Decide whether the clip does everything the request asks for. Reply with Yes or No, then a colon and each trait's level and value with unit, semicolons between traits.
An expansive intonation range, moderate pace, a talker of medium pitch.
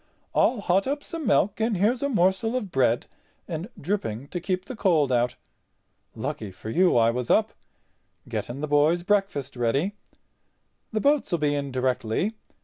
Yes: wide, 8.0 semitones; average, 155 wpm; medium, 175 Hz